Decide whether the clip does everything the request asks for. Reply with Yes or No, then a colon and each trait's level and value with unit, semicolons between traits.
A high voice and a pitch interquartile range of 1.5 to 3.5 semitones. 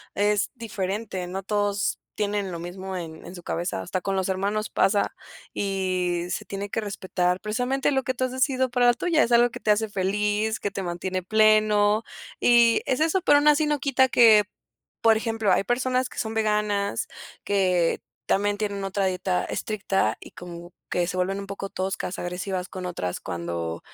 Yes: high, 200 Hz; average, 3.2 semitones